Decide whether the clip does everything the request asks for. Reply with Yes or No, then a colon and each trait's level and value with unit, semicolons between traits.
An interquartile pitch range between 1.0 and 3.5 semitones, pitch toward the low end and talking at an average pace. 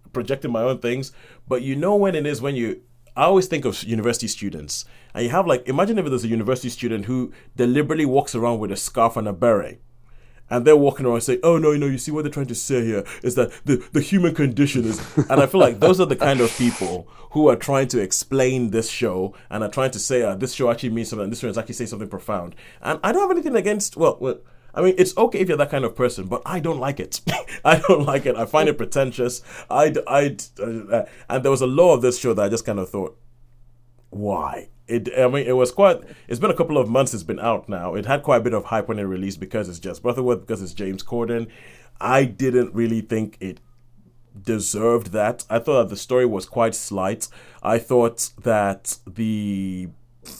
No: average, 3.2 semitones; low, 120 Hz; fast, 235 wpm